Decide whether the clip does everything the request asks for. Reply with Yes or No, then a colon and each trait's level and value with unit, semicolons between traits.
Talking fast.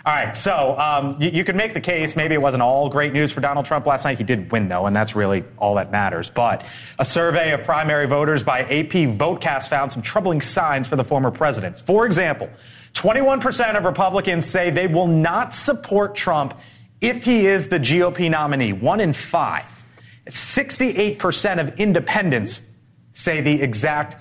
No: average, 185 wpm